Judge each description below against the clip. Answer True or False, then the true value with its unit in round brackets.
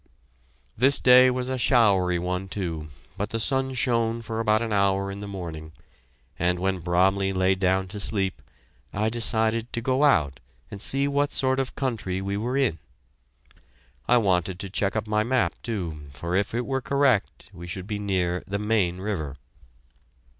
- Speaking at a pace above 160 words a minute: True (175 wpm)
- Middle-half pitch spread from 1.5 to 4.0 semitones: False (4.4 semitones)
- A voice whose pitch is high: False (100 Hz)